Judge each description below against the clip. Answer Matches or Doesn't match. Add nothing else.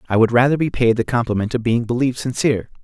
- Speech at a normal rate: Doesn't match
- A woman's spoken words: Doesn't match